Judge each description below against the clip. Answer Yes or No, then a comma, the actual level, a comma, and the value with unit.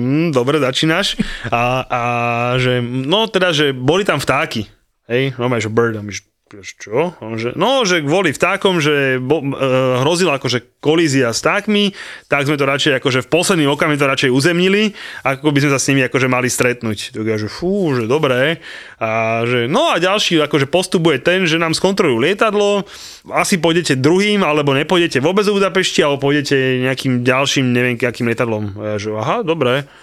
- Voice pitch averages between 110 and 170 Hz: Yes, medium, 140 Hz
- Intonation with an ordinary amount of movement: No, wide, 6.0 semitones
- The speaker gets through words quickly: Yes, fast, 170 wpm